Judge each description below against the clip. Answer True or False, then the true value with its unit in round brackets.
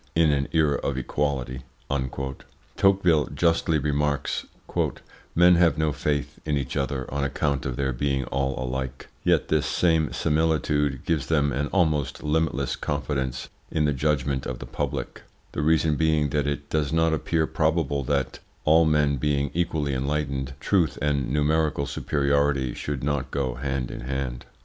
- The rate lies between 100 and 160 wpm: True (155 wpm)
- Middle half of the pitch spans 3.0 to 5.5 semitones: False (2.5 semitones)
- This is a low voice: True (70 Hz)